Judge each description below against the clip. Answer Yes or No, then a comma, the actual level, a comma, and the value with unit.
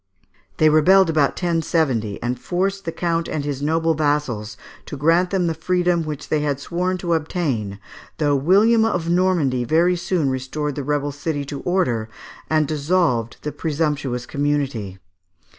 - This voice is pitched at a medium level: Yes, medium, 155 Hz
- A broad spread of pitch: No, average, 3.7 semitones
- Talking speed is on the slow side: No, average, 155 wpm